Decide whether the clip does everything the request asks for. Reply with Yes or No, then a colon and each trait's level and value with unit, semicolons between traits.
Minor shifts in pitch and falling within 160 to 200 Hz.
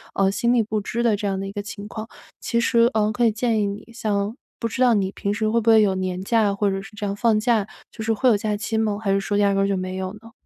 No: narrow, 2.2 semitones; high, 210 Hz